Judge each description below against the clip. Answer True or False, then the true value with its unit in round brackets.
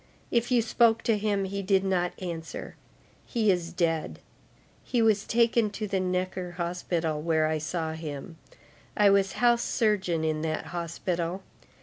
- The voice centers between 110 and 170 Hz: False (185 Hz)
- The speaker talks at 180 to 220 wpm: False (150 wpm)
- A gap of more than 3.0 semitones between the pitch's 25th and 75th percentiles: True (4.1 semitones)